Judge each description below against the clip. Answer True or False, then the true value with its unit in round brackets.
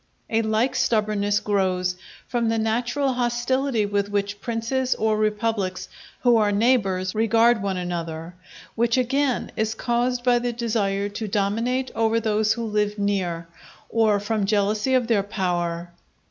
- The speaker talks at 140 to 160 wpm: True (145 wpm)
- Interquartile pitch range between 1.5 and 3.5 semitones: True (2.9 semitones)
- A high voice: True (215 Hz)